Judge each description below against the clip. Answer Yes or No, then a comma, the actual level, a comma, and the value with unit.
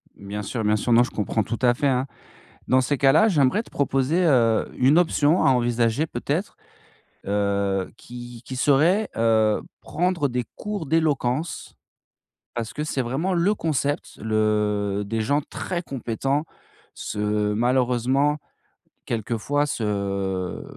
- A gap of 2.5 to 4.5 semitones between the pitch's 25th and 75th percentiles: No, average, 5.1 semitones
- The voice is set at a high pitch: No, low, 125 Hz